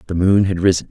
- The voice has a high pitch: No, very low, 90 Hz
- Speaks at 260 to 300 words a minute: Yes, fast, 265 wpm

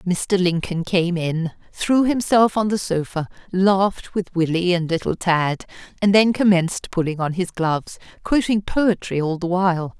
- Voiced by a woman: Yes, female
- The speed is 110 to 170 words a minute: Yes, average, 160 wpm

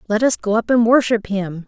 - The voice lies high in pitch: Yes, high, 220 Hz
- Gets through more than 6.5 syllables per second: No, 5.4 syllables/s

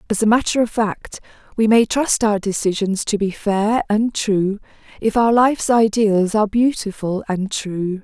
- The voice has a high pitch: Yes, high, 210 Hz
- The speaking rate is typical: Yes, average, 170 wpm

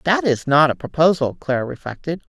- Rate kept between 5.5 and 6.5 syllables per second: Yes, 5.7 syllables/s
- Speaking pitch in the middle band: Yes, medium, 150 Hz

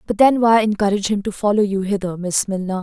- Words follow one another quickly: Yes, fast, 235 wpm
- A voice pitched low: No, high, 205 Hz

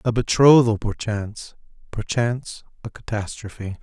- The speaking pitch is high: No, low, 110 Hz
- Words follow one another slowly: Yes, slow, 95 wpm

